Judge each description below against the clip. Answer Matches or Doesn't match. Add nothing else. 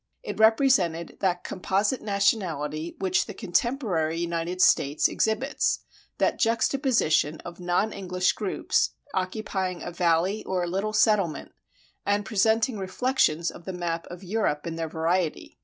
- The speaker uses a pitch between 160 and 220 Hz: Matches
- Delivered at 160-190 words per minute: Doesn't match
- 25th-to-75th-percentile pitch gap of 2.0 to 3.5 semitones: Doesn't match